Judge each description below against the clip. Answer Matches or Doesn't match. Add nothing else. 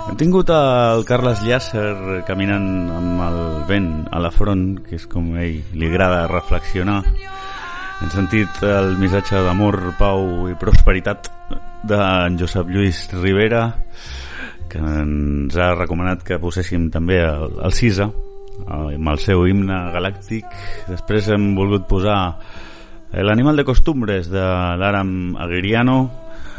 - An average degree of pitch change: Matches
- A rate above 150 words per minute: Doesn't match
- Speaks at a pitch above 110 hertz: Doesn't match